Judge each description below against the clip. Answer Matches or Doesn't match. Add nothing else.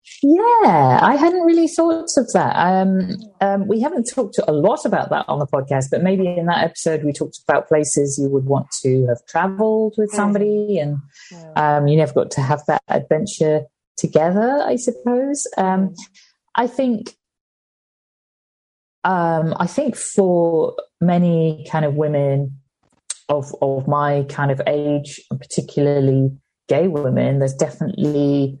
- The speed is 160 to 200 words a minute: Doesn't match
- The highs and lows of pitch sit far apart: Matches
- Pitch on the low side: Doesn't match